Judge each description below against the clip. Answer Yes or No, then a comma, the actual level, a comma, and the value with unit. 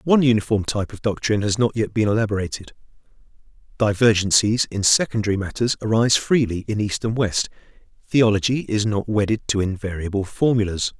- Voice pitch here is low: Yes, low, 105 Hz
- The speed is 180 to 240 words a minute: No, average, 145 wpm